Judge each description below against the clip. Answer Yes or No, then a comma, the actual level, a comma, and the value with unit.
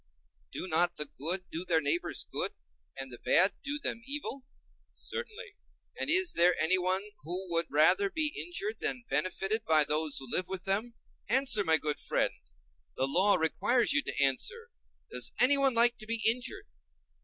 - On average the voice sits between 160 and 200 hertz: Yes, high, 190 Hz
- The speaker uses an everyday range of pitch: No, wide, 8.3 semitones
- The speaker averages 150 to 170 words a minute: Yes, average, 155 wpm